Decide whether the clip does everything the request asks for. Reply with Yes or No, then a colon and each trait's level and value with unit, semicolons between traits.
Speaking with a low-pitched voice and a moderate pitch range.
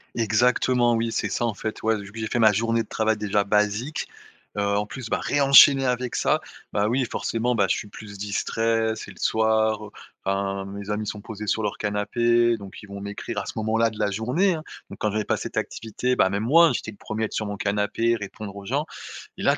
No: low, 110 Hz; narrow, 2.3 semitones